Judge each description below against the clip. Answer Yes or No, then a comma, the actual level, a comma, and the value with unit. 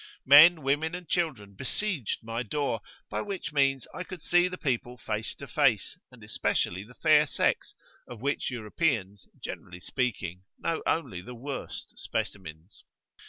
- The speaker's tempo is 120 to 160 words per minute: Yes, average, 150 wpm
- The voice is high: No, low, 130 Hz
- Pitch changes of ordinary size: No, wide, 6.9 semitones